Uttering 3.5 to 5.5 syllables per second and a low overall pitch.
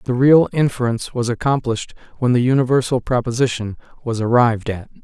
No: 6.1 syllables/s; low, 125 Hz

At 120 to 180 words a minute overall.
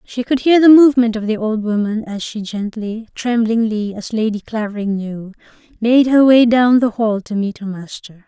No: average, 195 wpm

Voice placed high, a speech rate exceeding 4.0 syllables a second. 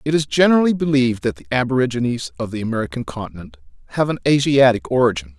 No: low, 125 Hz; 6.9 syllables/s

